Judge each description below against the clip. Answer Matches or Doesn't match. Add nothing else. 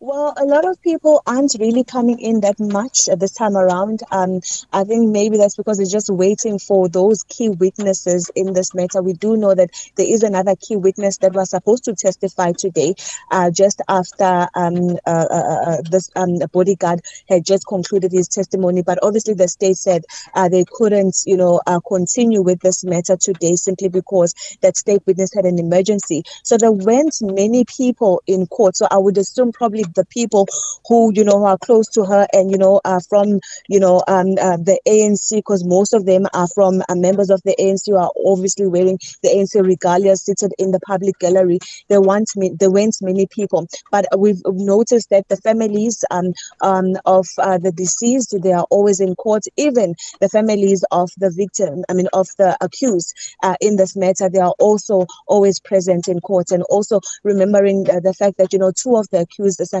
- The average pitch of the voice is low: Doesn't match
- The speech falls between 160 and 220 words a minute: Matches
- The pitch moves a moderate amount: Doesn't match